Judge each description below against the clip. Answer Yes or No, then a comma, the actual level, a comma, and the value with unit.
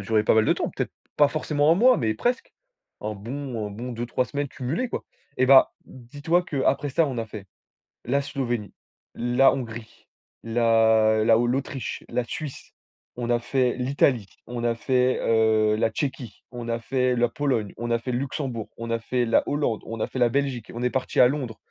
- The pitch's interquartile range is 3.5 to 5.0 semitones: No, average, 3.0 semitones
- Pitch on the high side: No, low, 120 Hz